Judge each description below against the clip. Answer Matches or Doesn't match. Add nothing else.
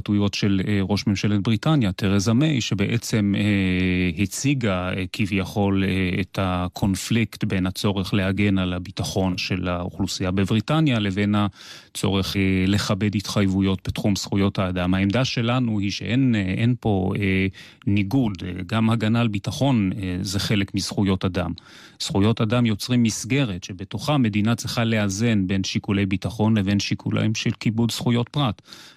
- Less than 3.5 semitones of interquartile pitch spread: Matches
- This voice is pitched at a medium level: Doesn't match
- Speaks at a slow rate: Doesn't match